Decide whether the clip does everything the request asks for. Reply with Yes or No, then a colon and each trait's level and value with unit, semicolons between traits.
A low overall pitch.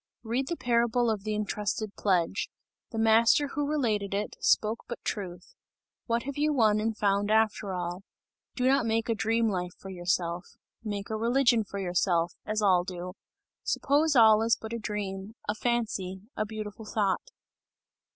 No: high, 215 Hz